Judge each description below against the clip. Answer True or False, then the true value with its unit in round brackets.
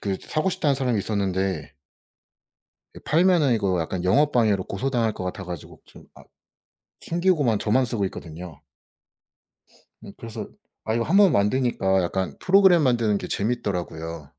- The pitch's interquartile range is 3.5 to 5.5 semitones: False (6.3 semitones)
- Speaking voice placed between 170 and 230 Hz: False (110 Hz)